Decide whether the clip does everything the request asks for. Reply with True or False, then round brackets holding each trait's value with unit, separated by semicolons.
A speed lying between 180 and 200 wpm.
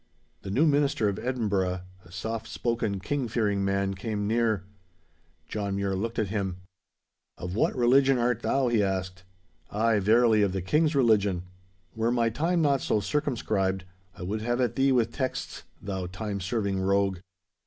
False (165 wpm)